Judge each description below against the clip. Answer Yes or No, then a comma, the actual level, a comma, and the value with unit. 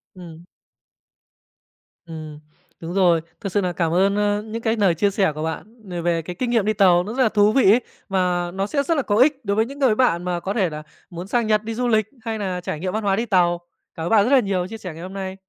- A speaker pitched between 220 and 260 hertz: No, high, 195 Hz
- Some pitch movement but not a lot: Yes, average, 3.9 semitones